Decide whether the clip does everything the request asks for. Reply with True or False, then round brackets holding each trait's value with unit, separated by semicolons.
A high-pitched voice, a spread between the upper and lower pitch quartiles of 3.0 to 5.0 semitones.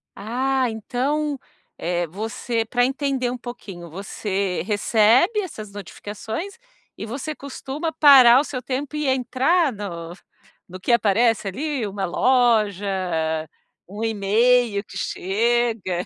True (235 Hz; 4.6 semitones)